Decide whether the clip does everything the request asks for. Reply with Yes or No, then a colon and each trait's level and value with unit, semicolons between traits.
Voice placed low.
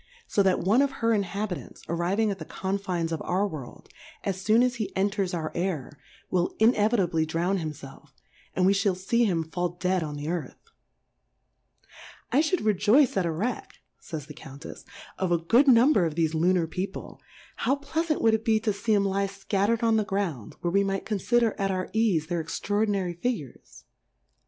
No: high, 195 Hz